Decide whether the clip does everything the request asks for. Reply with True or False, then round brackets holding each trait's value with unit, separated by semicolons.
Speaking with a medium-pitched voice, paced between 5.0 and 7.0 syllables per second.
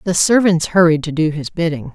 True (165 Hz; 5.5 syllables/s)